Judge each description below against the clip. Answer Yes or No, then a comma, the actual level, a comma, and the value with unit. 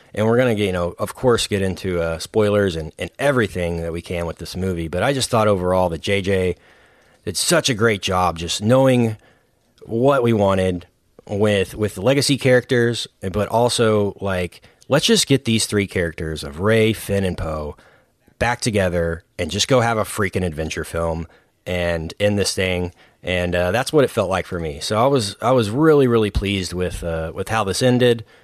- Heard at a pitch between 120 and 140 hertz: No, low, 100 Hz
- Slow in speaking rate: No, average, 195 wpm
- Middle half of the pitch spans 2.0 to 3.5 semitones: No, average, 4.6 semitones